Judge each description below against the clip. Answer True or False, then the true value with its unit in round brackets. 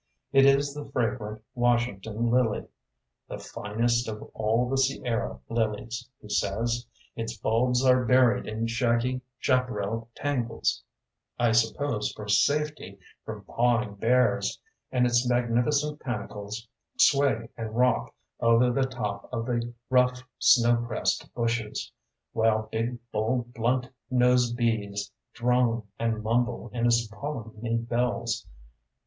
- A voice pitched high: False (120 Hz)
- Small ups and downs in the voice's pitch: True (2.0 semitones)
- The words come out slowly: True (120 wpm)